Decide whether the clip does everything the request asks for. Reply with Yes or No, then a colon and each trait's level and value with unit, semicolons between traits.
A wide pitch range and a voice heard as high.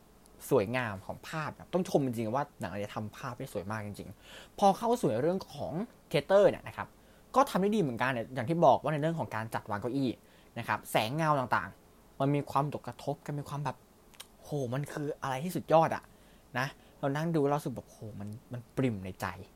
No: wide, 5.8 semitones; low, 135 Hz